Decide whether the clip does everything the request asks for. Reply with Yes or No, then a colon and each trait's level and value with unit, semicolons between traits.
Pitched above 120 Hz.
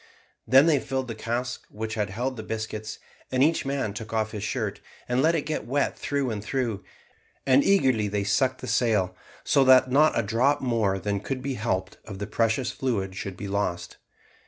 No: low, 115 Hz